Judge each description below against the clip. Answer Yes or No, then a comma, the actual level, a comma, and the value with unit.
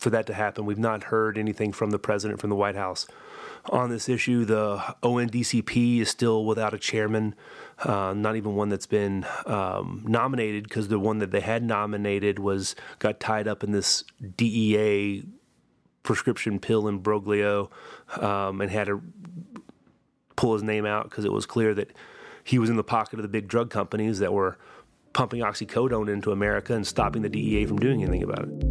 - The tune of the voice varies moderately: No, narrow, 1.7 semitones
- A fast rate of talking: No, average, 185 wpm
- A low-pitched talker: Yes, low, 105 Hz